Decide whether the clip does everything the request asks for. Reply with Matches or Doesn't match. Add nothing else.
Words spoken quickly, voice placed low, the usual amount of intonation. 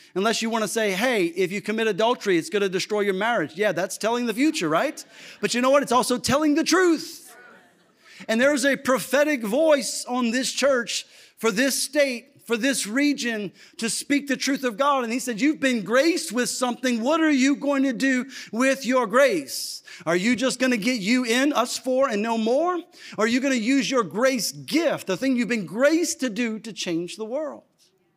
Doesn't match